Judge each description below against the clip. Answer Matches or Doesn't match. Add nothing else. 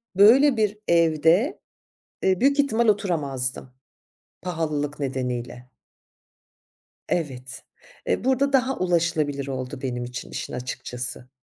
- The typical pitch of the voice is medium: Matches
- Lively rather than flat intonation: Matches